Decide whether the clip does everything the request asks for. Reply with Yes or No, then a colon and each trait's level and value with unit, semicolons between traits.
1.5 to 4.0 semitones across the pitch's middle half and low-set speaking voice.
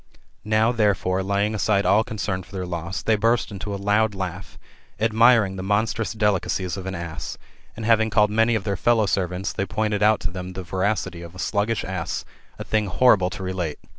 Yes: average, 2.7 semitones; low, 100 Hz